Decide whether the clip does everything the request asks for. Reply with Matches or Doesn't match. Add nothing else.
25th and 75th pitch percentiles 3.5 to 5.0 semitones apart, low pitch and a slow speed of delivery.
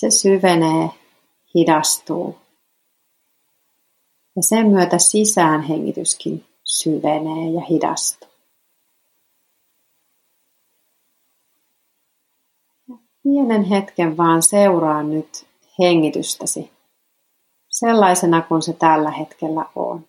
Doesn't match